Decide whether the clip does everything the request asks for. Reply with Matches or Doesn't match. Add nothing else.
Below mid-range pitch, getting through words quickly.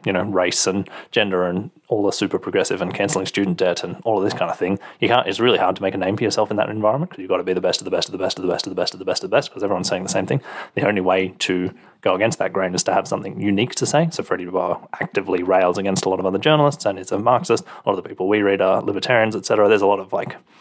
Matches